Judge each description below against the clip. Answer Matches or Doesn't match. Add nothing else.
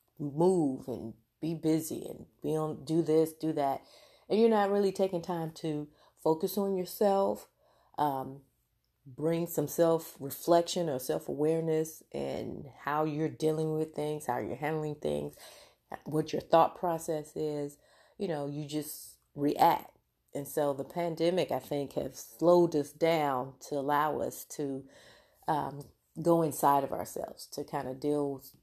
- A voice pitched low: Doesn't match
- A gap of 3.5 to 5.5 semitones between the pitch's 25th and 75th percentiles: Doesn't match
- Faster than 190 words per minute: Doesn't match